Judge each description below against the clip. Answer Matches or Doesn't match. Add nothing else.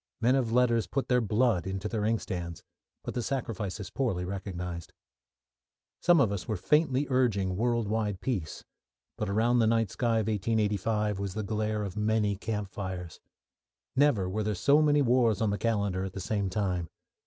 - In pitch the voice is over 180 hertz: Doesn't match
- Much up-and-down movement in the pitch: Doesn't match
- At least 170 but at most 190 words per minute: Matches